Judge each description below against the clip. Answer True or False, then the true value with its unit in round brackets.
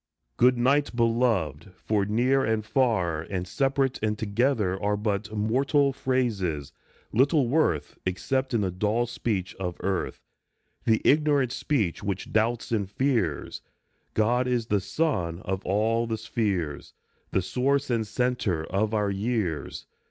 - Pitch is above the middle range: False (110 Hz)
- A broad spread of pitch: False (4.7 semitones)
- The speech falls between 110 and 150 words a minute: True (140 wpm)